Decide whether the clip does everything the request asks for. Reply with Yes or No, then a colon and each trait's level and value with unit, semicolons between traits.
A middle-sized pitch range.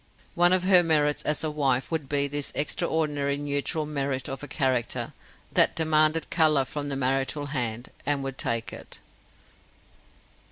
No: narrow, 2.3 semitones